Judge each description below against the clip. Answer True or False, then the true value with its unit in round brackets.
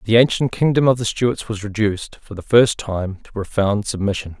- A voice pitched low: True (110 Hz)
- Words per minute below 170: False (205 wpm)